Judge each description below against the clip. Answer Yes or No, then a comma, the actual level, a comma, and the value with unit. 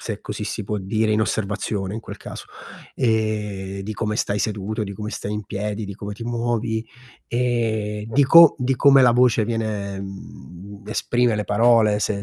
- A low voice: Yes, low, 110 Hz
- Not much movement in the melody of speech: Yes, narrow, 2.3 semitones